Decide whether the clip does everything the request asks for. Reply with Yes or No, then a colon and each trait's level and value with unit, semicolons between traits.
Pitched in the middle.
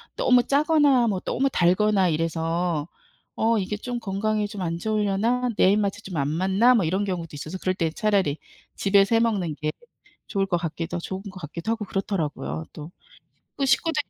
No: high, 195 Hz